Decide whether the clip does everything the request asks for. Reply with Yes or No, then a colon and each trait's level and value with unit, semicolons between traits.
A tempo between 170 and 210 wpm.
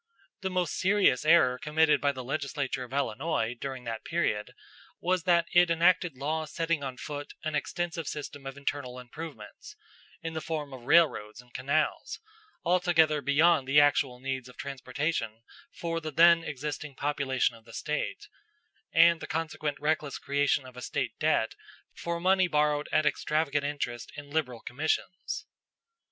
No: average, 155 wpm